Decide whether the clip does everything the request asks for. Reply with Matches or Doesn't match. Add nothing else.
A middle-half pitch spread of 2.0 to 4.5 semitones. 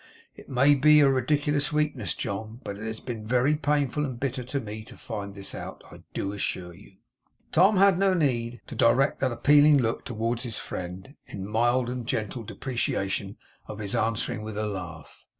Doesn't match